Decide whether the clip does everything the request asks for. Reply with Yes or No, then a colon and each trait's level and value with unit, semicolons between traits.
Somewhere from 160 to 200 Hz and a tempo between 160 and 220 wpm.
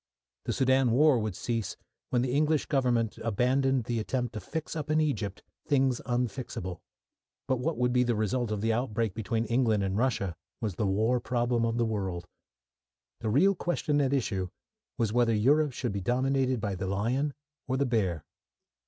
No: low, 120 Hz; average, 180 wpm